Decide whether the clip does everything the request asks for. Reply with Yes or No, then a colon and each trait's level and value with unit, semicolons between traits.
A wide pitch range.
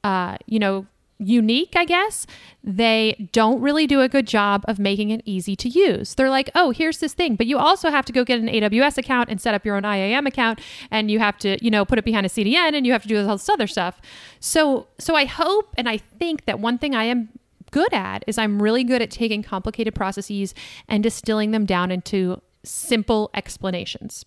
No: average, 4.4 semitones